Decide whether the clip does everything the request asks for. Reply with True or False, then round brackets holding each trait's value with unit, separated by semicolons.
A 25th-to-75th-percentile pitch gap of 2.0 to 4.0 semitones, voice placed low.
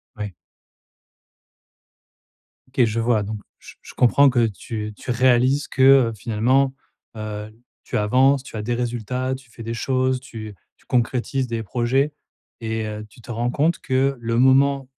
True (2.9 semitones; 120 Hz)